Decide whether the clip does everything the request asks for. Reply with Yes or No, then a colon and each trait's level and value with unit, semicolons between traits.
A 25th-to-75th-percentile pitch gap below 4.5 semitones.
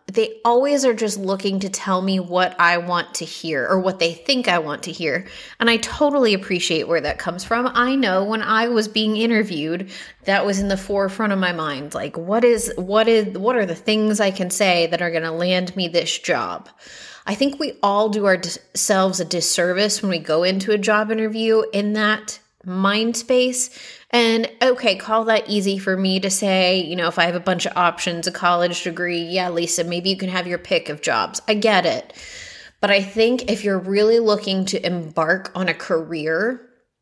Yes: average, 3.7 semitones